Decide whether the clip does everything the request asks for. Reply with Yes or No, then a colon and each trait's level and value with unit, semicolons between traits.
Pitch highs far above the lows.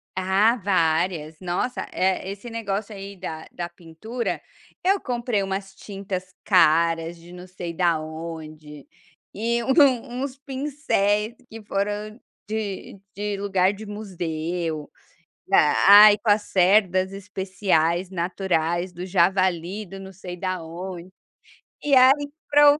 No: average, 3.5 semitones